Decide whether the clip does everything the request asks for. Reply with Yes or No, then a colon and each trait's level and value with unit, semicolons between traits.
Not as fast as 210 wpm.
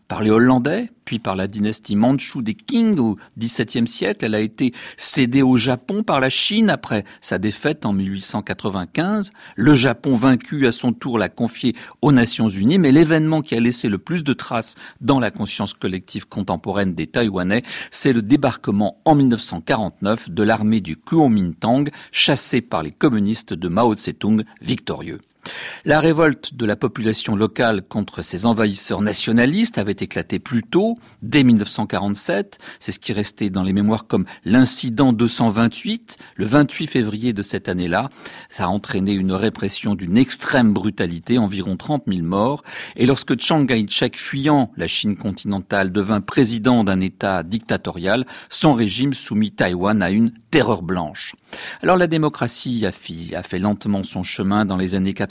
Yes: average, 160 wpm